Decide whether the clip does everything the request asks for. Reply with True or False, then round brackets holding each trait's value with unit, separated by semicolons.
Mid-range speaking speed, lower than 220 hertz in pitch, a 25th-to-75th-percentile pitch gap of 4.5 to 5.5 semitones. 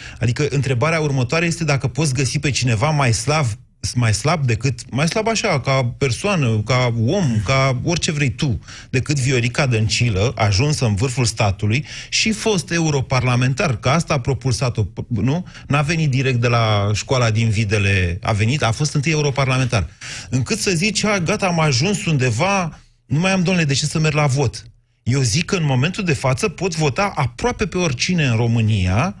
False (175 wpm; 135 Hz; 4.8 semitones)